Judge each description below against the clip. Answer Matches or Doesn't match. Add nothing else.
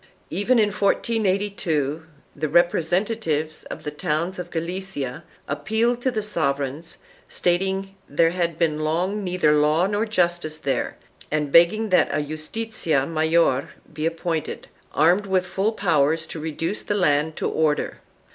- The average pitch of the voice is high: Doesn't match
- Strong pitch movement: Doesn't match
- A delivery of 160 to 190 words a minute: Doesn't match